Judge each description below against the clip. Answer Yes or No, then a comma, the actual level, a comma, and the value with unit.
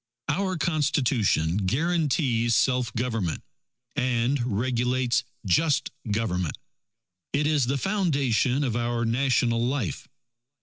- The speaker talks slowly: Yes, slow, 95 wpm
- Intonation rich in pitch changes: No, average, 3.7 semitones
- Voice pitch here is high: No, low, 125 Hz